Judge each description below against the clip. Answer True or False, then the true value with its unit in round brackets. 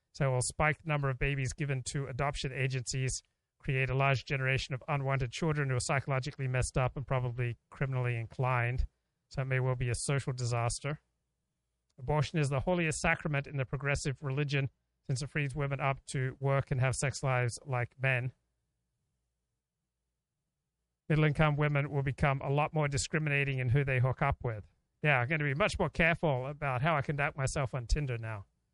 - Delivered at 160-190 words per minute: True (185 wpm)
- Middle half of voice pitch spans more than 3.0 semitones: False (2.4 semitones)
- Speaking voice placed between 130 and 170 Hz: True (135 Hz)